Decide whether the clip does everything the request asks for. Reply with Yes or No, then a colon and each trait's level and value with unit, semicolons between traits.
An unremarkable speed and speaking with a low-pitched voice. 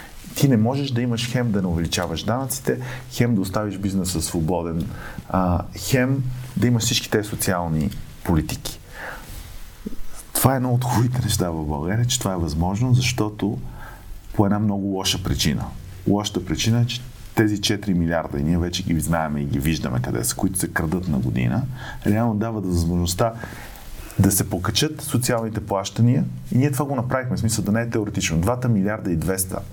No: fast, 175 wpm; low, 105 Hz